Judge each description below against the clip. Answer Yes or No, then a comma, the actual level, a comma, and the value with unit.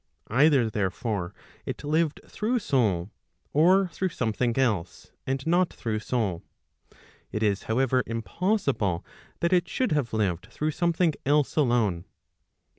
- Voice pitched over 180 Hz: No, low, 130 Hz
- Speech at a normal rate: No, slow, 125 wpm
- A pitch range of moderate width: No, wide, 7.1 semitones